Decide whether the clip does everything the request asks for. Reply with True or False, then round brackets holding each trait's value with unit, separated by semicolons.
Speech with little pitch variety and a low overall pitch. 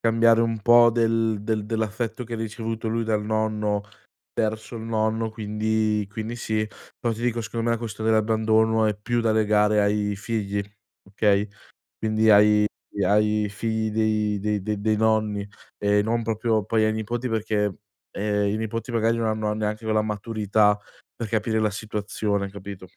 True (1.2 semitones; 110 Hz)